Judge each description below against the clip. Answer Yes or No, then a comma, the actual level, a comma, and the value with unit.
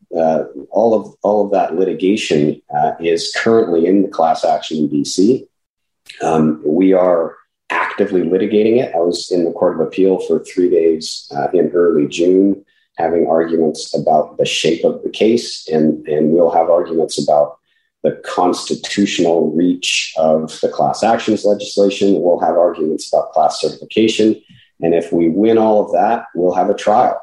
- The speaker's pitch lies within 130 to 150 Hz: No, very low, 95 Hz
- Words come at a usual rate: Yes, average, 165 wpm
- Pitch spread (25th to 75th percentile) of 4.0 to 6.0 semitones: Yes, average, 4.5 semitones